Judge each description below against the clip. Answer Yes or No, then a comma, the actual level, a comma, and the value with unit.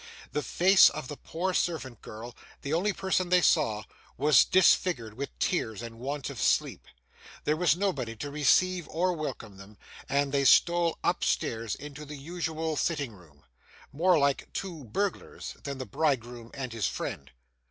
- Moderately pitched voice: Yes, medium, 145 Hz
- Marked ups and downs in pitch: Yes, wide, 6.4 semitones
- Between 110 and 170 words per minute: Yes, average, 160 wpm